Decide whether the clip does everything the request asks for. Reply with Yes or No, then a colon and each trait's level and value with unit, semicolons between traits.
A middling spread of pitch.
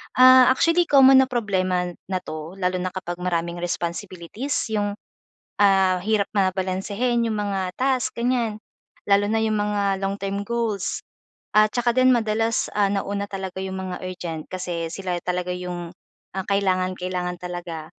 Yes: average, 3.2 semitones